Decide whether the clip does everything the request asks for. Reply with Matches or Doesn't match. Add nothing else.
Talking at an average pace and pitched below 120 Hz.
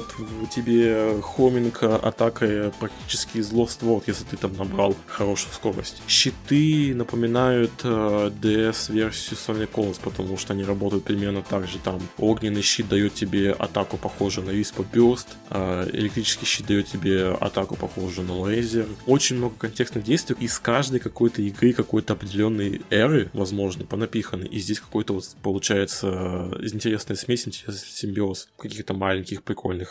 Matches